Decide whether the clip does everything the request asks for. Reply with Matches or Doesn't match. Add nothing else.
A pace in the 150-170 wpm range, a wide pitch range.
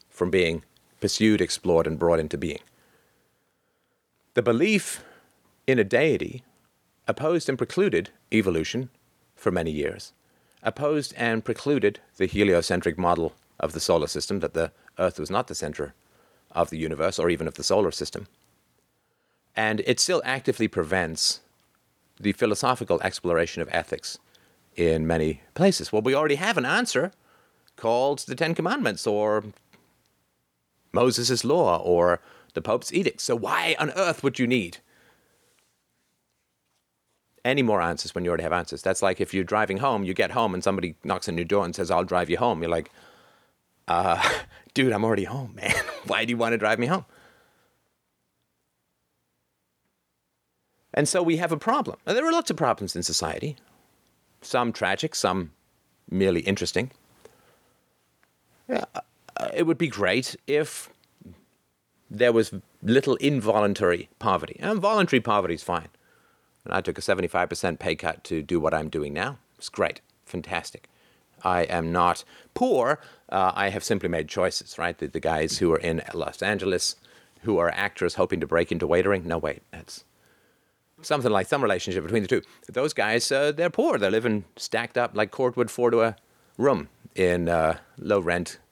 Matches